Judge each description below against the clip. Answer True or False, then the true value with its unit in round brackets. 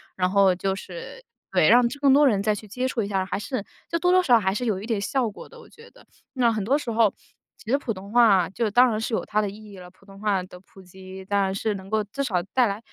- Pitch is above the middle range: True (210 Hz)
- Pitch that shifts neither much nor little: True (3.9 semitones)